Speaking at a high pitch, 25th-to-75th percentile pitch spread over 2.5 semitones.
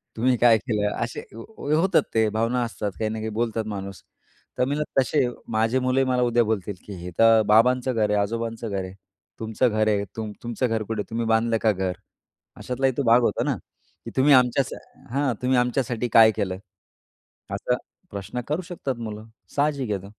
No: low, 115 Hz; average, 2.9 semitones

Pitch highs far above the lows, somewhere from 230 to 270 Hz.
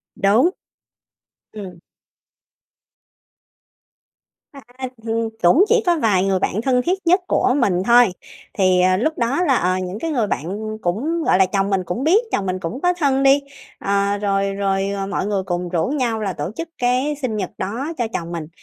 No: wide, 6.1 semitones; high, 210 Hz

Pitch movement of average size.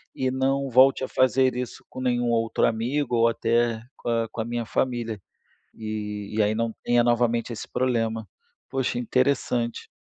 No: narrow, 2.1 semitones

